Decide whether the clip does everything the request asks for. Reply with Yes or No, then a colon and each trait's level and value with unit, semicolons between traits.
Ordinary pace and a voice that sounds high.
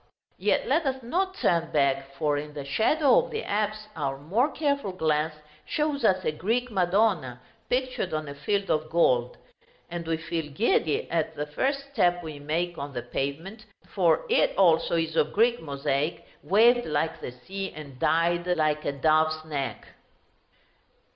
No: average, 165 wpm; medium, 165 Hz